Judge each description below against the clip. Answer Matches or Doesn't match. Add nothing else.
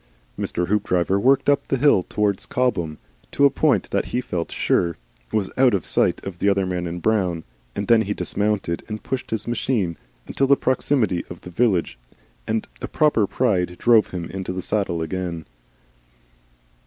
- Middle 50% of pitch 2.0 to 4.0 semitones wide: Doesn't match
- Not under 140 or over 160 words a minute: Doesn't match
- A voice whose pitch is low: Matches